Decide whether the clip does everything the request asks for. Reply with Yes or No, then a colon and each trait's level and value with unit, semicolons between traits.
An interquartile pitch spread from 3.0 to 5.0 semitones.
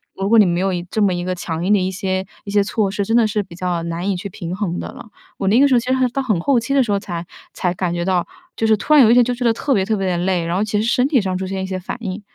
Yes: average, 3.6 semitones